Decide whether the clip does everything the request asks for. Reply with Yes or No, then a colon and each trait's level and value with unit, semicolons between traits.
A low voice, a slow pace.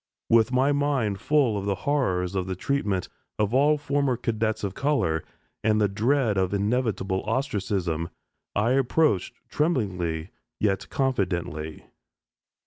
Yes: low, 105 Hz; slow, 130 wpm